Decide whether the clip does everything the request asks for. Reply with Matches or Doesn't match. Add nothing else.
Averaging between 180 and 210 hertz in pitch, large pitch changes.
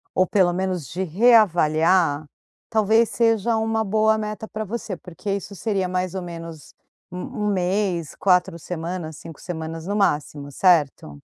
Doesn't match